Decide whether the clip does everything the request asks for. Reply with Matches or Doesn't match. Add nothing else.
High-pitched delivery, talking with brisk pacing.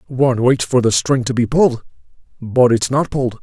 Doesn't match